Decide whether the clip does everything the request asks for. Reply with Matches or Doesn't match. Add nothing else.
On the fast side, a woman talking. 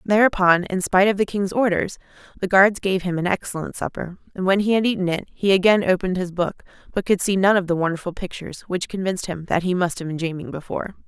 Matches